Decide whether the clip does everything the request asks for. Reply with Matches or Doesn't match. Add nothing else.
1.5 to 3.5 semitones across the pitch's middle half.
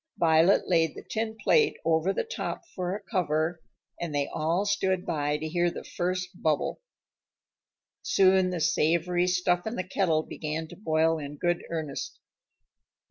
Matches